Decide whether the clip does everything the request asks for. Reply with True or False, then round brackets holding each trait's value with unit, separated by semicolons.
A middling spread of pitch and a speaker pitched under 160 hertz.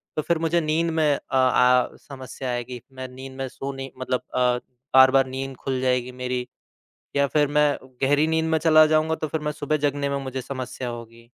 True (3.2 semitones; 135 Hz)